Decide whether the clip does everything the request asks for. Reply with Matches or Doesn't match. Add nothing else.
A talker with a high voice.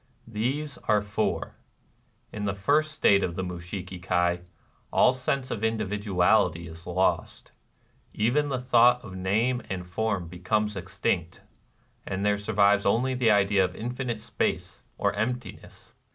Doesn't match